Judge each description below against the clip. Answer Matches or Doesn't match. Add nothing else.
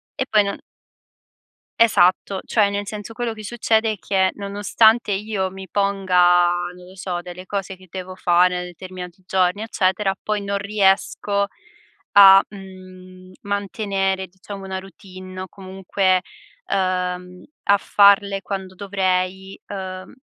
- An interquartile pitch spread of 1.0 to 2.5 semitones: Matches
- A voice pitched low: Doesn't match